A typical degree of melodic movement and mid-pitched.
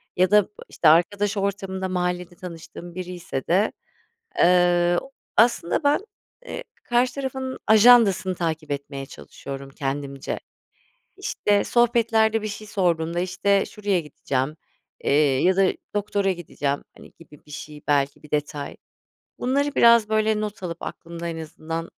Yes: average, 4.8 semitones; medium, 180 Hz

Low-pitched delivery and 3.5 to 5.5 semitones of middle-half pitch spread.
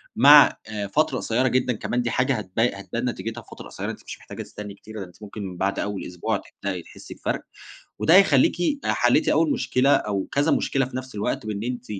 Yes: low, 115 Hz; average, 4.2 semitones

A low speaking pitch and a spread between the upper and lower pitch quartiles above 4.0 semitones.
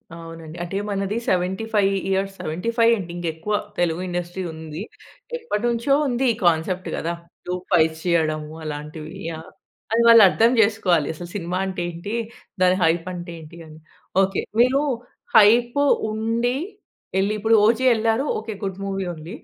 No: high, 190 Hz; average, 4.9 semitones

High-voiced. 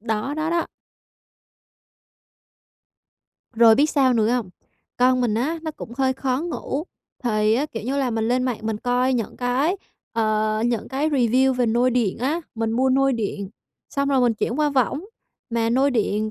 Yes: very high, 250 Hz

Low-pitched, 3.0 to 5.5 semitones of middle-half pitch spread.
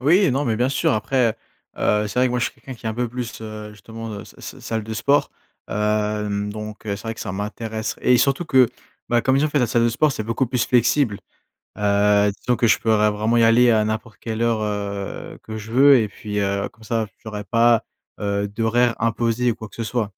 No: low, 110 Hz; narrow, 2.4 semitones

